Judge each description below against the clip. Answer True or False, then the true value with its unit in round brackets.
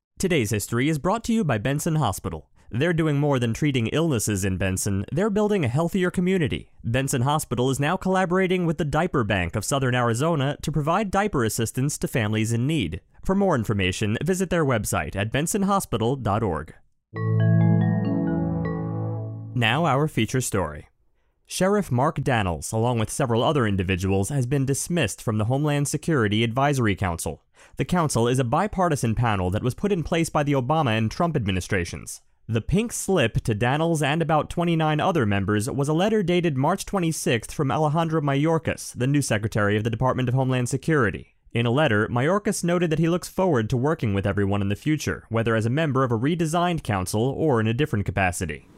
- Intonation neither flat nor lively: False (6.8 semitones)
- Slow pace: False (180 wpm)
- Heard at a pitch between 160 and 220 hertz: False (135 Hz)